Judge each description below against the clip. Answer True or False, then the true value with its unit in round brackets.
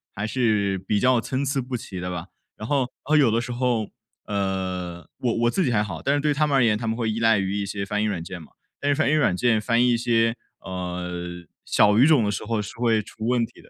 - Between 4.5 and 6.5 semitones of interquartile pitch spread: False (4.1 semitones)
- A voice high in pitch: False (110 Hz)